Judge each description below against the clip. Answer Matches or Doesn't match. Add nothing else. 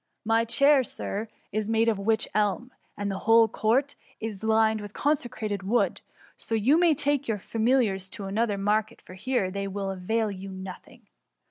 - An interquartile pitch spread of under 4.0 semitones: Matches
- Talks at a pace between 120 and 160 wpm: Doesn't match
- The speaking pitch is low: Doesn't match